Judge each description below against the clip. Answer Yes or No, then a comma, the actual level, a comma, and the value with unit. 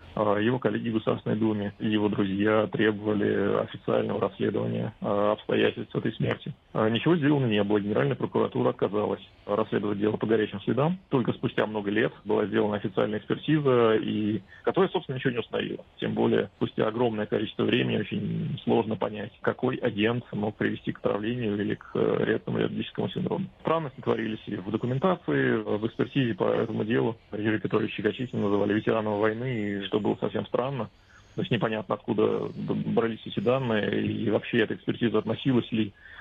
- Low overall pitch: Yes, low, 110 Hz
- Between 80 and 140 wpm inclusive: No, average, 155 wpm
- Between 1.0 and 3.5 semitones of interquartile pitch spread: Yes, narrow, 2.6 semitones